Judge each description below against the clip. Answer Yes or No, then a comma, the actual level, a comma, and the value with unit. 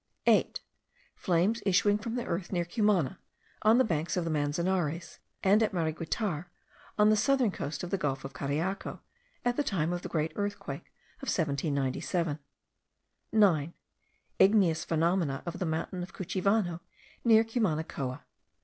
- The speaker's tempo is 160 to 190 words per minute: No, average, 145 wpm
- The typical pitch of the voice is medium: Yes, medium, 175 Hz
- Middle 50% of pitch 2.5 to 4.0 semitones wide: No, average, 4.6 semitones